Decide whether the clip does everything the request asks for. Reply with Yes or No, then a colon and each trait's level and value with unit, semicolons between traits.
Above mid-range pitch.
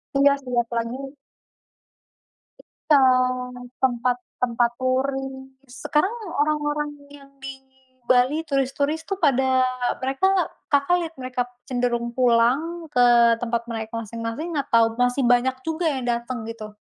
Yes: very high, 255 Hz